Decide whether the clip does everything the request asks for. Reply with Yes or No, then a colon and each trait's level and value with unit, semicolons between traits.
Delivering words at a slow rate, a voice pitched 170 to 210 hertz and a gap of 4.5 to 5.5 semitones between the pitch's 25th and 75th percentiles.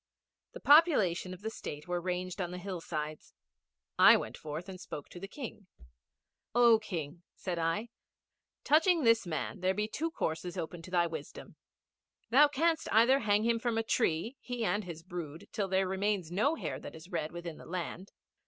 No: average, 180 wpm; medium, 185 Hz; average, 4.9 semitones